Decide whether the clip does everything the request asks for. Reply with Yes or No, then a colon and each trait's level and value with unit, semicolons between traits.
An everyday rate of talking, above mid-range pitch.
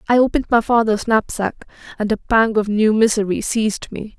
Yes: average, 185 wpm; high, 220 Hz